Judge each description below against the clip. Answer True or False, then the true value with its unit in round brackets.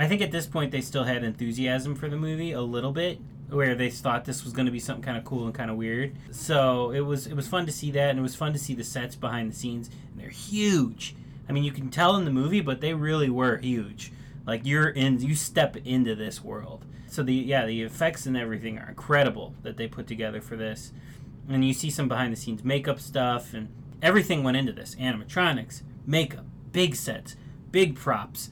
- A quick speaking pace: True (230 wpm)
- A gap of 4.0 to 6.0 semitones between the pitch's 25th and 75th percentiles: False (2.9 semitones)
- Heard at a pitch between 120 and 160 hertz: True (135 Hz)